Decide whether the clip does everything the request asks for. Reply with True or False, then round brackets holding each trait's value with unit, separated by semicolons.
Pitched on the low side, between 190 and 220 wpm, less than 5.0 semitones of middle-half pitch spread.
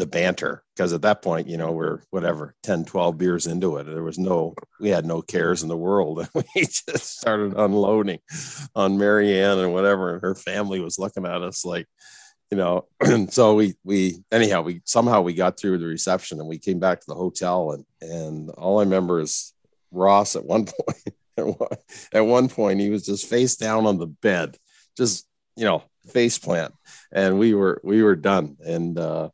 True (95 Hz; 200 wpm; 3.3 semitones)